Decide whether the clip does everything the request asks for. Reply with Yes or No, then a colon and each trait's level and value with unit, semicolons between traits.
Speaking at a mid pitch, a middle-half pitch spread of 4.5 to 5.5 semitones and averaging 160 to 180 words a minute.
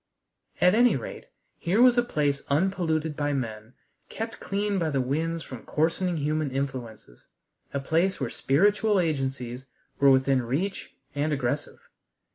No: medium, 150 Hz; average, 5.2 semitones; average, 140 wpm